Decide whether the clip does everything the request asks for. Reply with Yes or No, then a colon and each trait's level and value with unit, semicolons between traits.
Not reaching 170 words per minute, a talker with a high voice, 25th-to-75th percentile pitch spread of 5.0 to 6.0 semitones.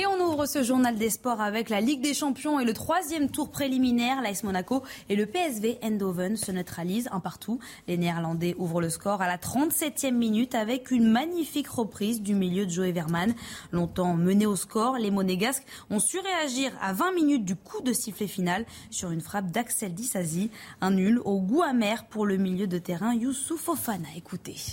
No: average, 195 wpm; high, 220 Hz; wide, 5.5 semitones